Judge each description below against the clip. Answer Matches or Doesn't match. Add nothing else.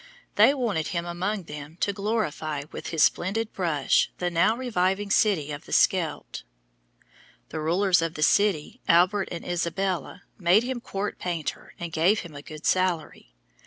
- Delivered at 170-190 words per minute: Doesn't match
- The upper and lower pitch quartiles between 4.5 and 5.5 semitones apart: Doesn't match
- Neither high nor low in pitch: Matches